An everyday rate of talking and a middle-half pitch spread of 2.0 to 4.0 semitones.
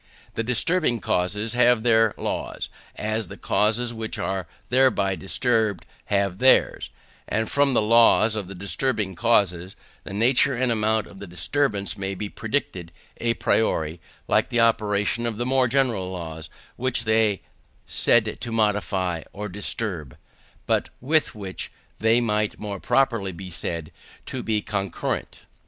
Yes: average, 145 wpm; average, 3.4 semitones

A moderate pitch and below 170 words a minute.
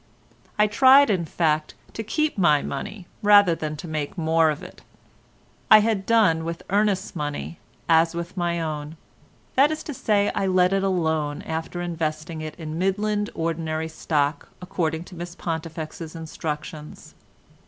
Yes: medium, 170 Hz; average, 155 wpm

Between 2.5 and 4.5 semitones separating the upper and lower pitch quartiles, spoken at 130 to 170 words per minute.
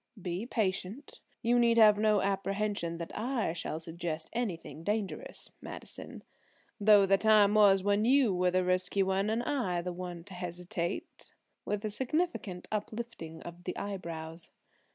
Yes: average, 3.4 semitones; average, 150 wpm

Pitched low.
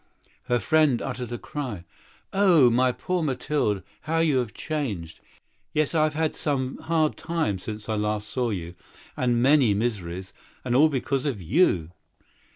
Yes: low, 125 Hz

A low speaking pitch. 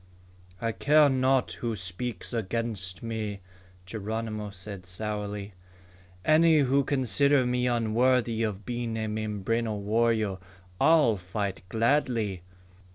Yes: low, 115 Hz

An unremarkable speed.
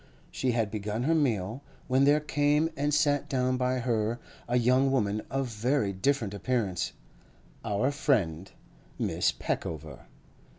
No: slow, 130 wpm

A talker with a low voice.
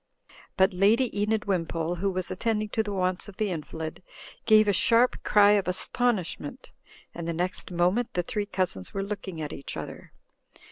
No: high, 190 Hz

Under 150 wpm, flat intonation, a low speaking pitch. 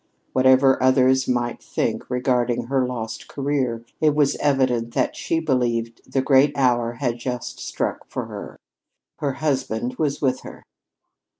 Yes: average, 140 wpm; narrow, 2.2 semitones; low, 130 Hz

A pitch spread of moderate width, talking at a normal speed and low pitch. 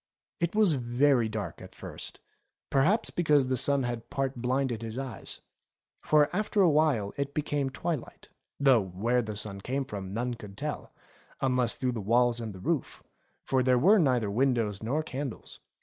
Yes: average, 3.9 semitones; average, 175 wpm; low, 125 Hz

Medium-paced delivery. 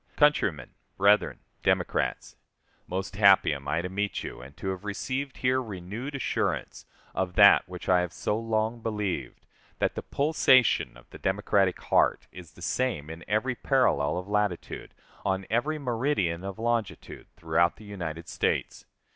Yes: average, 155 wpm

